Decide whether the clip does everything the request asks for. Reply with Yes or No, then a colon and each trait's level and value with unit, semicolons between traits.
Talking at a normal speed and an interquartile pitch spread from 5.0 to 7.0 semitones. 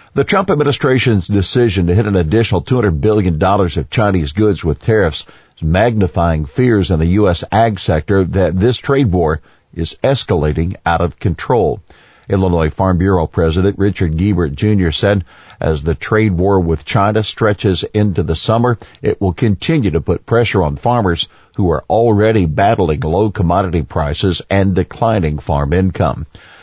No: average, 155 wpm; average, 4.1 semitones